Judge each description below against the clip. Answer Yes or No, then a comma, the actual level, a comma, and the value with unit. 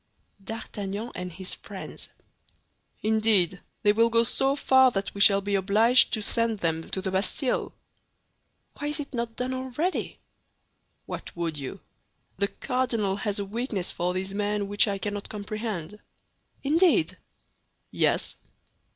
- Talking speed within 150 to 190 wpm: No, average, 140 wpm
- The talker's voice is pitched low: No, high, 210 Hz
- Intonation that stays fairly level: No, average, 3.6 semitones